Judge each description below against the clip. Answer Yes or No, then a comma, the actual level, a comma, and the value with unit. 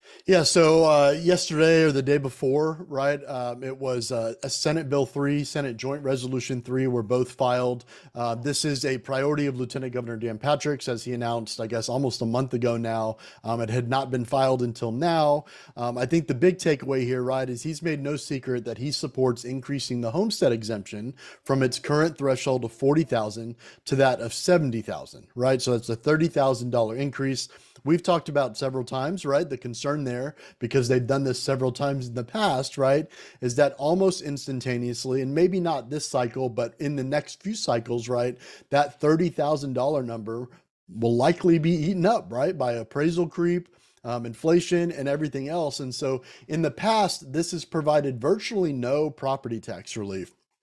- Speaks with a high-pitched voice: No, low, 135 Hz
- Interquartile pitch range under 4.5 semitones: Yes, average, 3.5 semitones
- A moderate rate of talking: Yes, average, 180 wpm